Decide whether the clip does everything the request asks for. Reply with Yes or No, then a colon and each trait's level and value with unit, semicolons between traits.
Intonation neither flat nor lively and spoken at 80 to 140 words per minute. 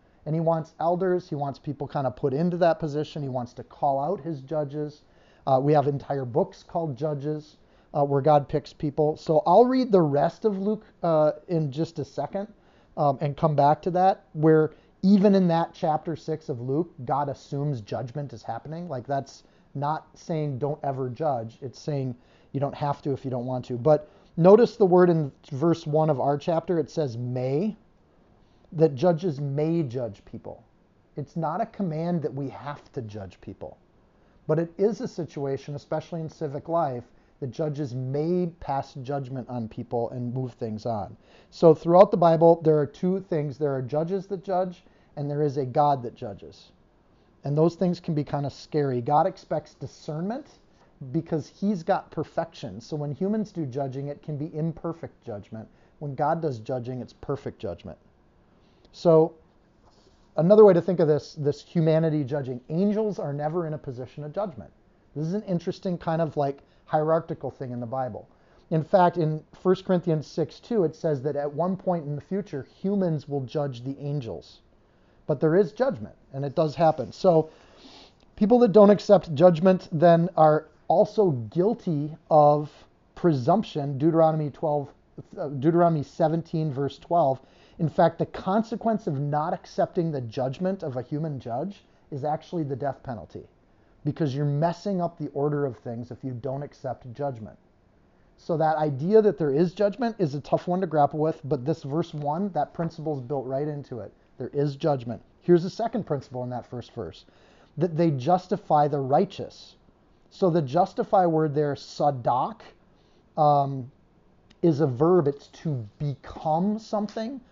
No: average, 3.6 semitones; average, 175 wpm